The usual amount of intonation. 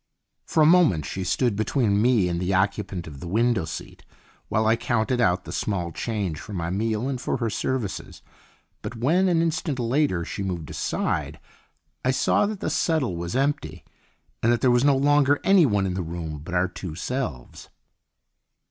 No: wide, 6.8 semitones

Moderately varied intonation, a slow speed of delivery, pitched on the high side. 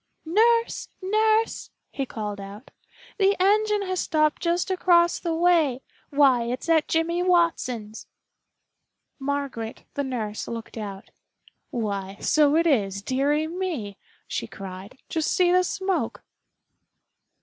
No: wide, 7.7 semitones; slow, 120 wpm; very high, 300 Hz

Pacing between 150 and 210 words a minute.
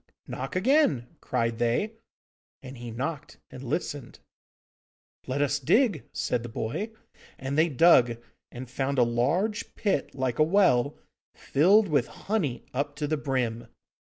No: average, 140 wpm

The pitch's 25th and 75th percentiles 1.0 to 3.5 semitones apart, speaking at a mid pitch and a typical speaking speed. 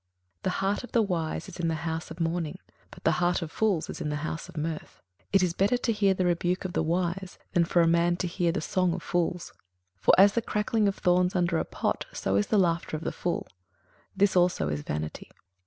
No: narrow, 2.5 semitones; medium, 175 Hz; fast, 250 wpm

